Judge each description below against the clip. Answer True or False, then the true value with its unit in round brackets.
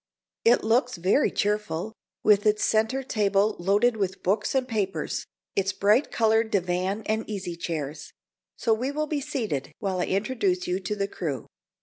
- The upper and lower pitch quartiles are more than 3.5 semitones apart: False (3.1 semitones)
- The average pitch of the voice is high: True (210 Hz)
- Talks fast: False (160 wpm)